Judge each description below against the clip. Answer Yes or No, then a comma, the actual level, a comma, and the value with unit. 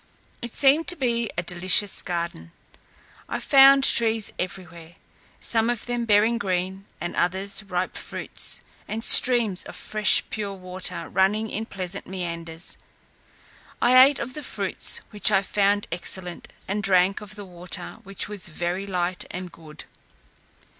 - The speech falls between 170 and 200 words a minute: No, average, 145 wpm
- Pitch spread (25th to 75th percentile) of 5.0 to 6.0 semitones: No, average, 3.7 semitones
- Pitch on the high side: Yes, high, 195 Hz